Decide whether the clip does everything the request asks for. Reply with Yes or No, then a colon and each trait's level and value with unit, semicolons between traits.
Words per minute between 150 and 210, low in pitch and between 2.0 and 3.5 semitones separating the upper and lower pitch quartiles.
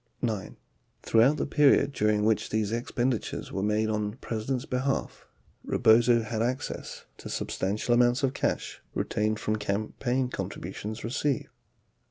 No: average, 140 wpm; low, 115 Hz; average, 2.8 semitones